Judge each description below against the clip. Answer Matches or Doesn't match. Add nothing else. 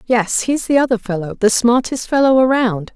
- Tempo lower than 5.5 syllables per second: Matches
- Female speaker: Matches